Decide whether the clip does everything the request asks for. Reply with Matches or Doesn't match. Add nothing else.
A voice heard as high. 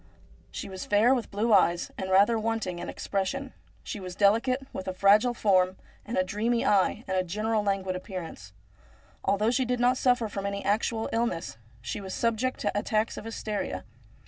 Matches